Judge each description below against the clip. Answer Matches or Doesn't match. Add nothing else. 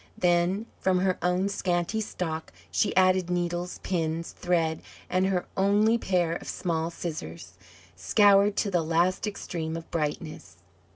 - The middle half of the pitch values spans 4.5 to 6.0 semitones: Doesn't match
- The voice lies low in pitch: Doesn't match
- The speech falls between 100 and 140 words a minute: Matches